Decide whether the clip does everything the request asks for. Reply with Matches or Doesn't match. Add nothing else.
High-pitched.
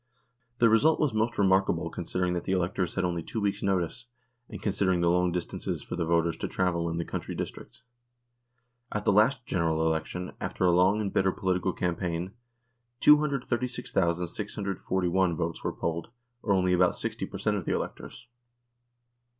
Doesn't match